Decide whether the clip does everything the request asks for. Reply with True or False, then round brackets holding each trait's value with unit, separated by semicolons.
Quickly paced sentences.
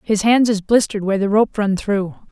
True (235 wpm)